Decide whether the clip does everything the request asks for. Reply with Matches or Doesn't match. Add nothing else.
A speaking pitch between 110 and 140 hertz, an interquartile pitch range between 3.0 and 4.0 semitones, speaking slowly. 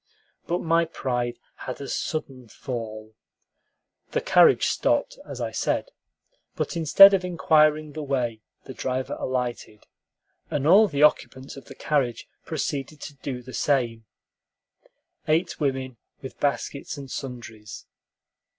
Matches